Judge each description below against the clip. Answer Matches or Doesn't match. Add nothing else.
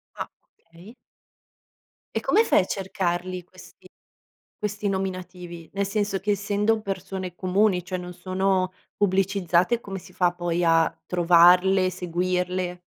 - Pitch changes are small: Matches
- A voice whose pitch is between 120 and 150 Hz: Doesn't match